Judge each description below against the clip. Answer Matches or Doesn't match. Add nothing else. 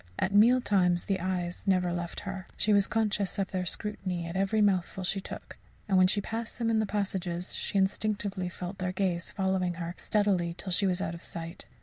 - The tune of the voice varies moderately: Doesn't match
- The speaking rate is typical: Doesn't match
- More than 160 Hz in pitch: Matches